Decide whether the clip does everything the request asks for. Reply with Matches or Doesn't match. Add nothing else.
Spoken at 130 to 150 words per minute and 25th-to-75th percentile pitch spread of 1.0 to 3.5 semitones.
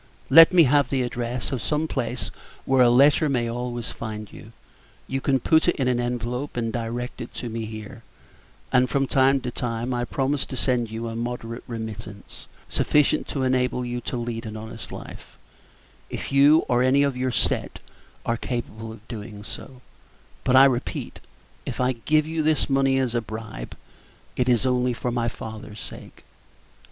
Doesn't match